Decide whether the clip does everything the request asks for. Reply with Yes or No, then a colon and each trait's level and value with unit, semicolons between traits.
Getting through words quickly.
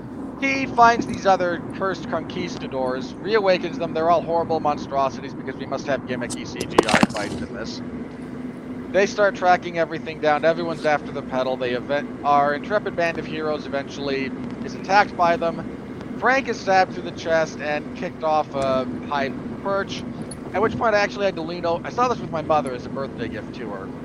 No: average, 185 wpm